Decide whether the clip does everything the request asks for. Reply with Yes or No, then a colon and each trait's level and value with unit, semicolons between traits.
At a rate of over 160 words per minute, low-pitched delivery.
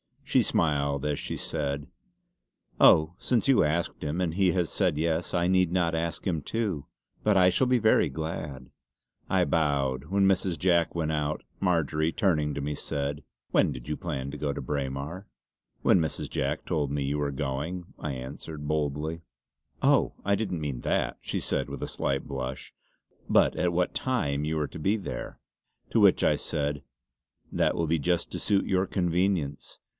Yes: average, 180 wpm; very low, 80 Hz